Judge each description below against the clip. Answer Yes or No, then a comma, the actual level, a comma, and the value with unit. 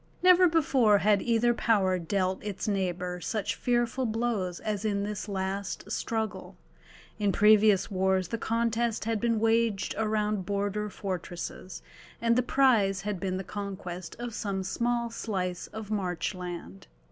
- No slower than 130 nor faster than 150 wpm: Yes, average, 140 wpm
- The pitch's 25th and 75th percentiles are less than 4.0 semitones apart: Yes, average, 3.2 semitones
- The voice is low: No, high, 210 Hz